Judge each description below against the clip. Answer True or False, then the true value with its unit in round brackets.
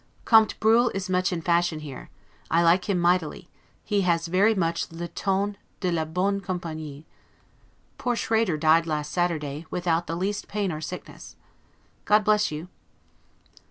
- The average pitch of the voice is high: False (175 Hz)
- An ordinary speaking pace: True (155 wpm)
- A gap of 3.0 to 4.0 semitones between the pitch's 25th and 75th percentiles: True (3.3 semitones)